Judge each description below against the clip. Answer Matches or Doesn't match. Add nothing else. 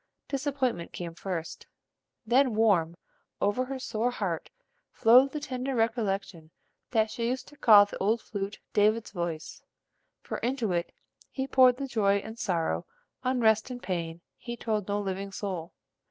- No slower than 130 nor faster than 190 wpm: Matches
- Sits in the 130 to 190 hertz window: Doesn't match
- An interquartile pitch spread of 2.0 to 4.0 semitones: Doesn't match